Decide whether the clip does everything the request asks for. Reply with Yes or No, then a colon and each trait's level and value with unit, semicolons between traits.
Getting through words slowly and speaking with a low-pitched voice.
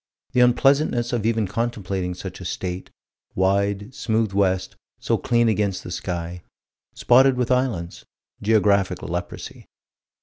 Yes: slow, 125 wpm; low, 100 Hz